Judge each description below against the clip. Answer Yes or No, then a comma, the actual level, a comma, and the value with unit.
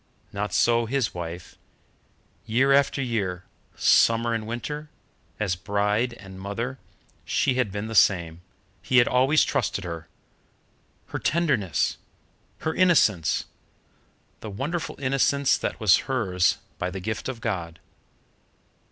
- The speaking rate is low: Yes, slow, 125 wpm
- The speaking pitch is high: No, low, 110 Hz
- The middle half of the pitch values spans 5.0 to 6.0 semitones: Yes, wide, 5.5 semitones